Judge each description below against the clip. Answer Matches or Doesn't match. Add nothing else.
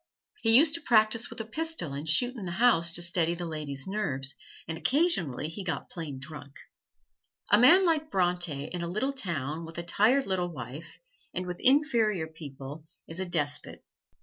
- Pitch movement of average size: Doesn't match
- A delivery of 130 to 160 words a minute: Doesn't match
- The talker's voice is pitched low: Doesn't match